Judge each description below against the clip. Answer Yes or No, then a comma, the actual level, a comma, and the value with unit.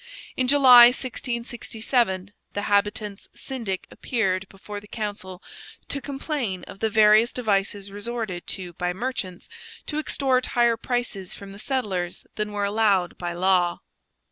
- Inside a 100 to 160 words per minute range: Yes, slow, 135 wpm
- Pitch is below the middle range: No, high, 210 Hz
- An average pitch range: Yes, average, 4.0 semitones